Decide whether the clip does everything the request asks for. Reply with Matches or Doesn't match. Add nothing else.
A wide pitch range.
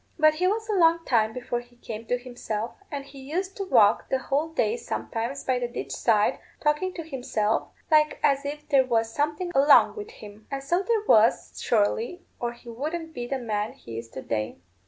Matches